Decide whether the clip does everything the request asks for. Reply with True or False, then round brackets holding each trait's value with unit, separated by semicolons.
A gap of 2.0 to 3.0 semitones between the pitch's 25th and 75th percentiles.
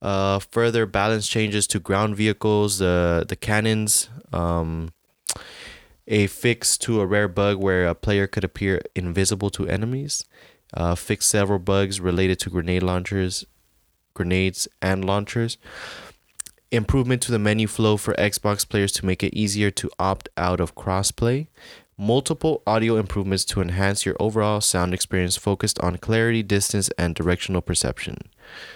True (2.4 semitones)